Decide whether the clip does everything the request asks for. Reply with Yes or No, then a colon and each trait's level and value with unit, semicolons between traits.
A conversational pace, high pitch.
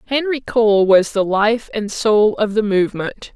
Yes: average, 180 wpm; high, 215 Hz